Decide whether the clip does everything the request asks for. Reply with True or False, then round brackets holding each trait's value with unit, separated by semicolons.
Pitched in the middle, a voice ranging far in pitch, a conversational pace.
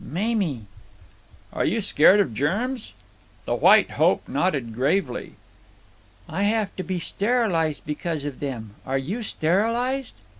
False (180 Hz; 7.2 semitones; 125 wpm)